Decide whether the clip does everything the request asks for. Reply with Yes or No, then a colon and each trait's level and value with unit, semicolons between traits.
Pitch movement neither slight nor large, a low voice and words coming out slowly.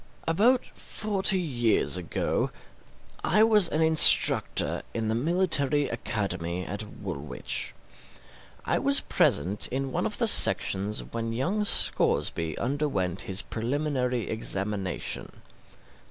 No: wide, 8.2 semitones; low, 120 Hz; slow, 110 wpm